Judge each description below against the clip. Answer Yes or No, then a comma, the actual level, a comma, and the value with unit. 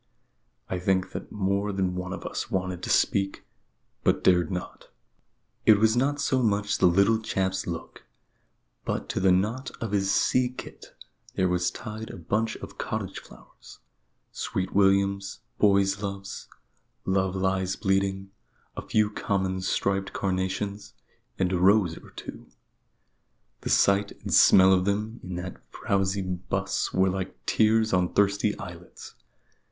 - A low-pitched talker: Yes, very low, 95 Hz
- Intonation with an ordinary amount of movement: No, narrow, 1.7 semitones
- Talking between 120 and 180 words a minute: Yes, average, 145 wpm